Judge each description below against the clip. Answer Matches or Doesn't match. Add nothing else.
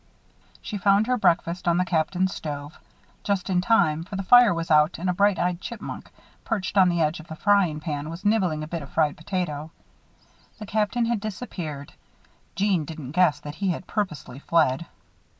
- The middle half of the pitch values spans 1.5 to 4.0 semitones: Doesn't match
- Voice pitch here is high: Doesn't match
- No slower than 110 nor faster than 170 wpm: Doesn't match